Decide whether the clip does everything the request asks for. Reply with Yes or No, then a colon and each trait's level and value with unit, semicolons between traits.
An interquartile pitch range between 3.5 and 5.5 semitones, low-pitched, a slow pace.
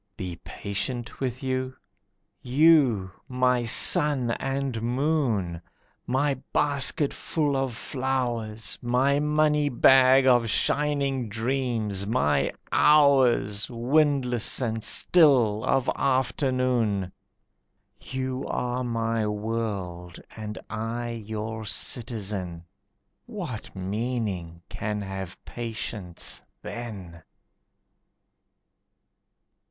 Yes: average, 3.8 semitones; low, 120 Hz; slow, 80 wpm